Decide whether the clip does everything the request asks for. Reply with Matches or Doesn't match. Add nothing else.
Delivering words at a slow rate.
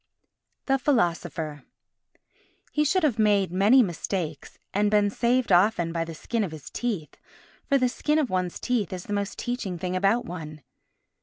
Doesn't match